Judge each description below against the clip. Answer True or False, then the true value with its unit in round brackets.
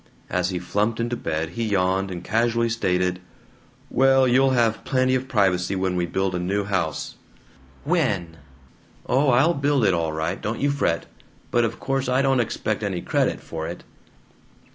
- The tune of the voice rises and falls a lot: True (6.0 semitones)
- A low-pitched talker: True (105 Hz)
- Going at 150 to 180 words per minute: True (170 wpm)